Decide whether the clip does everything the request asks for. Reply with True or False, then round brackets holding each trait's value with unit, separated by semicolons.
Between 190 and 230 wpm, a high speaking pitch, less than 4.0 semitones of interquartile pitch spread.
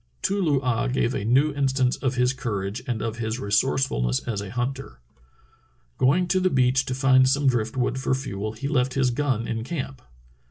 False (195 wpm; 130 Hz; 2.9 semitones)